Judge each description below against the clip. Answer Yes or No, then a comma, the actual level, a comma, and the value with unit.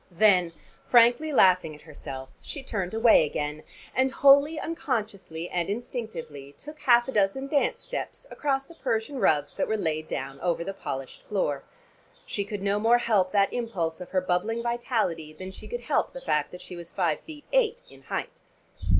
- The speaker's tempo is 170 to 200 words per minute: Yes, average, 180 wpm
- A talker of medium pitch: No, high, 205 Hz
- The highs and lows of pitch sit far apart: Yes, wide, 6.6 semitones